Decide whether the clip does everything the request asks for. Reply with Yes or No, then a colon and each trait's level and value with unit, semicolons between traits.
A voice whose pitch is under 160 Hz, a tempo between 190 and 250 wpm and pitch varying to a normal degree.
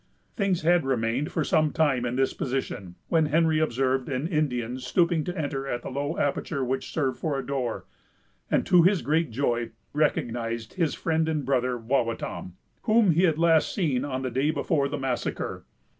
No: medium, 140 Hz; average, 180 wpm; average, 4.2 semitones